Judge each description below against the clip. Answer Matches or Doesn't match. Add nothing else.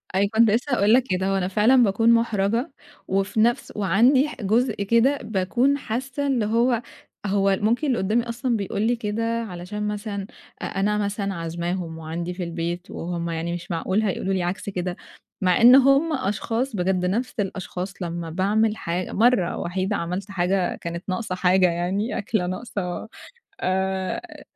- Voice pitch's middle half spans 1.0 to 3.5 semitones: Doesn't match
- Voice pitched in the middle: Doesn't match